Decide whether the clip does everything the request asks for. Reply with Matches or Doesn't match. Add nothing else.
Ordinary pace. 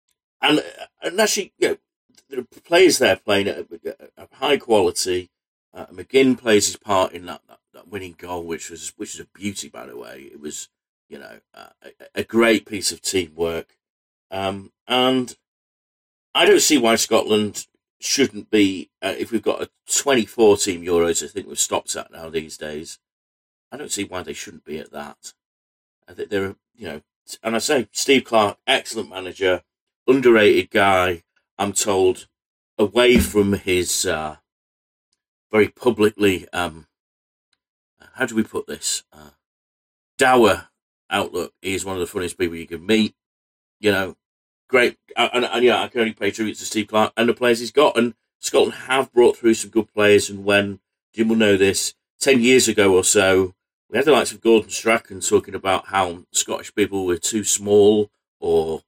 Matches